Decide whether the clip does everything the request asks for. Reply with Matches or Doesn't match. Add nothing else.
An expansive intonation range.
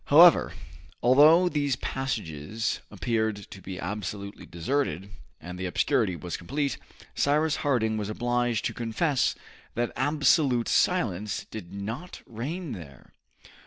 Matches